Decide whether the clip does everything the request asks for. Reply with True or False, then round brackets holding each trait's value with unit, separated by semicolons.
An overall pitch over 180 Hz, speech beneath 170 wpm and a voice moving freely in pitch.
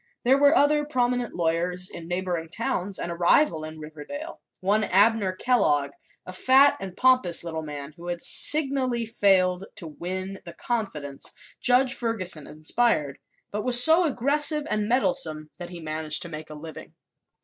True (190 Hz; 160 wpm; 7.3 semitones)